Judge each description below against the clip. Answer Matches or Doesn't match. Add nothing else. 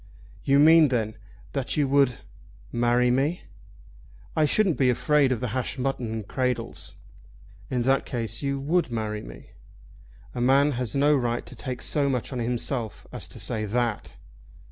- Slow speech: Doesn't match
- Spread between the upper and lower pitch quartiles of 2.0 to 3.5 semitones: Matches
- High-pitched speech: Doesn't match